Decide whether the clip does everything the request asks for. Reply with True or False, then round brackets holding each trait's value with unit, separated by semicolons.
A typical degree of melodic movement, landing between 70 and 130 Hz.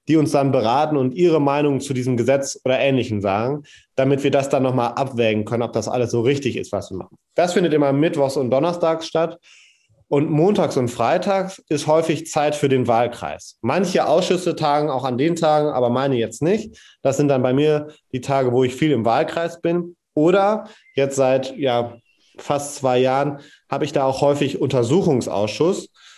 False (3.3 semitones; 140 Hz)